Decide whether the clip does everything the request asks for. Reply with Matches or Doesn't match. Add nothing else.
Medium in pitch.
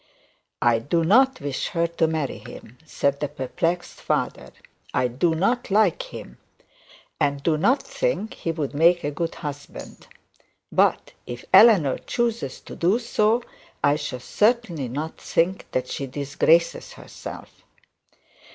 Matches